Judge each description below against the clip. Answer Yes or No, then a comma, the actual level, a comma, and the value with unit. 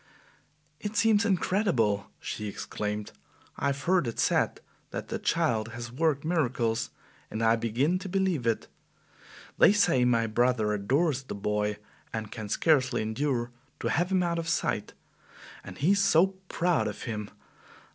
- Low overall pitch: Yes, low, 125 Hz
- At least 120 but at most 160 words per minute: Yes, average, 155 wpm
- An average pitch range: No, wide, 7.6 semitones